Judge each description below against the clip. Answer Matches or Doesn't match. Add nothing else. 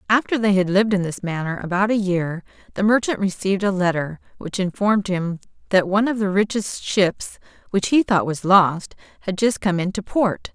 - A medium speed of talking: Matches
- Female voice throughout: Matches